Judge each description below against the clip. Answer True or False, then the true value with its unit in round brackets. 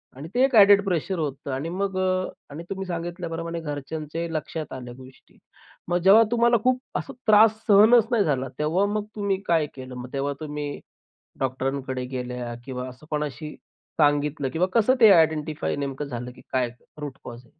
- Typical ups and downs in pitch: False (6.1 semitones)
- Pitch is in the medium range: True (155 Hz)